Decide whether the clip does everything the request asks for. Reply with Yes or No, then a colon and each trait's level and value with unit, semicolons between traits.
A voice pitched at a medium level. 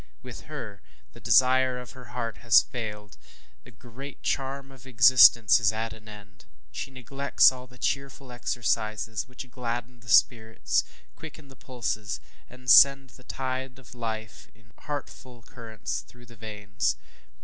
No: low, 120 Hz